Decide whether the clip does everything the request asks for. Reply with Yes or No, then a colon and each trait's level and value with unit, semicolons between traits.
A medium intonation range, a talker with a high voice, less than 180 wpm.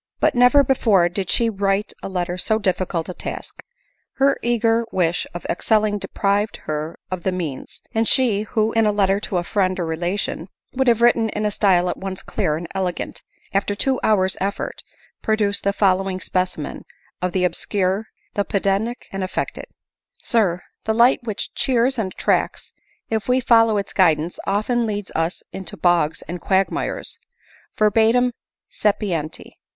Yes: average, 3.4 semitones; high, 200 Hz; average, 165 wpm